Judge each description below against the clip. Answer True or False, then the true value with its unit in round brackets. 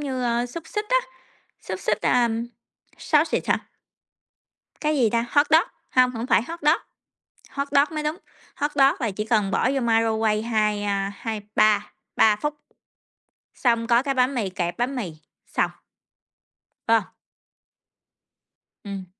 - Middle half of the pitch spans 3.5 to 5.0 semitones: True (4.6 semitones)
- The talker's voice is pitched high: True (235 Hz)